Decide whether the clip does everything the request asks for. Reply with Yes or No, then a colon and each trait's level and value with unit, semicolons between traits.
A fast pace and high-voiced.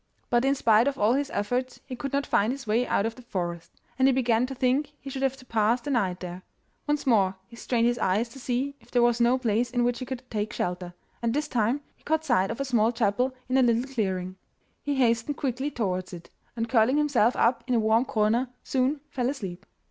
Yes: fast, 240 wpm; high, 240 Hz